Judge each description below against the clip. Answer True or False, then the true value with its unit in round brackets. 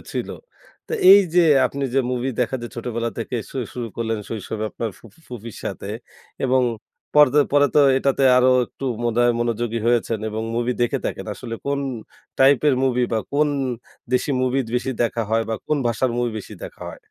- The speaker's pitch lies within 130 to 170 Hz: False (120 Hz)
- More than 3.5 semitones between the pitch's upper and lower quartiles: False (2.6 semitones)